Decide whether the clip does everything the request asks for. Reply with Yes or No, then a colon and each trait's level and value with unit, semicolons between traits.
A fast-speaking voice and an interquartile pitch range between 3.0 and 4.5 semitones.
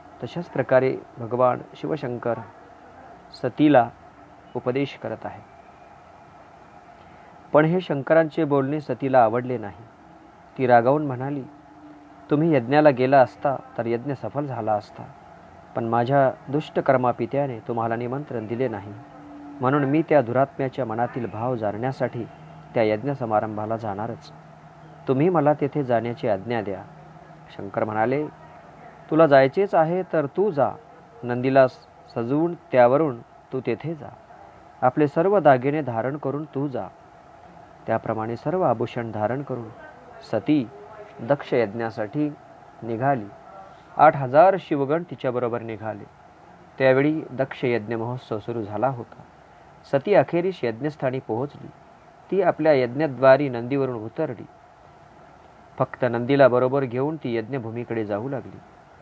No: average, 110 wpm; average, 4.0 semitones